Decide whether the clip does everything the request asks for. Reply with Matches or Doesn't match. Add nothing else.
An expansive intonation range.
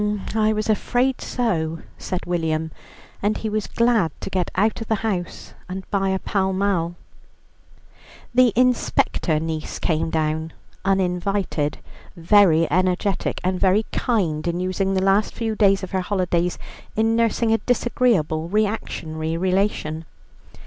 Doesn't match